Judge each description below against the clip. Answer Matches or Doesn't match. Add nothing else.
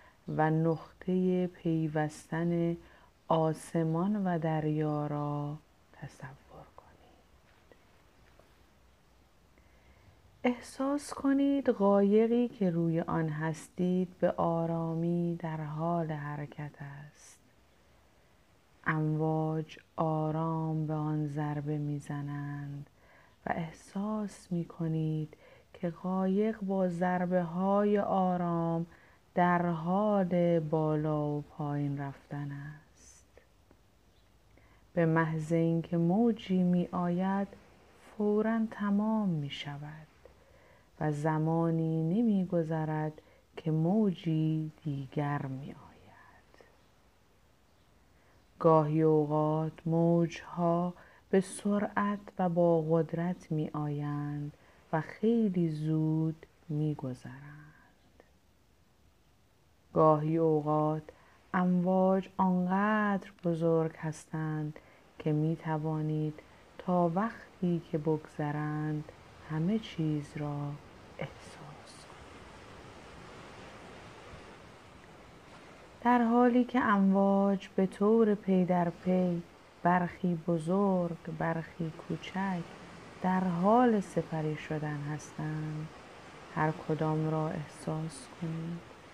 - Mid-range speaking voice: Matches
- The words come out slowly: Matches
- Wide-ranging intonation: Doesn't match